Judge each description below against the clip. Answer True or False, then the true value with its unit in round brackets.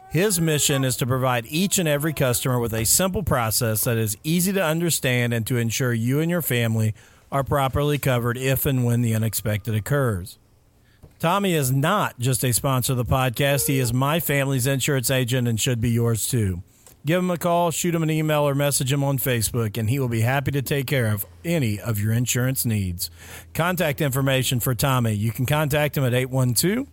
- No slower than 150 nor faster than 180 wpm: False (205 wpm)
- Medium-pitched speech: False (130 Hz)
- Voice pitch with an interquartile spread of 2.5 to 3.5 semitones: False (4.0 semitones)